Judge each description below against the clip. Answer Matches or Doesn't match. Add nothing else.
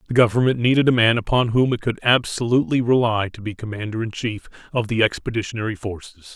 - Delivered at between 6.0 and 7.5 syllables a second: Matches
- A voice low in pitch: Matches